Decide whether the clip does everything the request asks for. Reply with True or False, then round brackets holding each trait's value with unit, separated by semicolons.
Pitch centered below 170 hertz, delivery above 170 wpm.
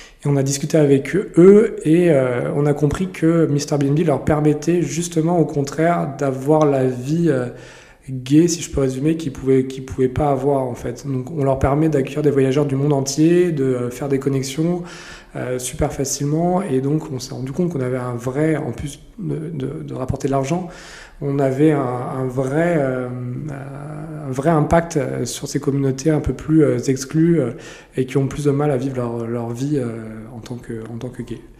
True (140 Hz; 200 wpm)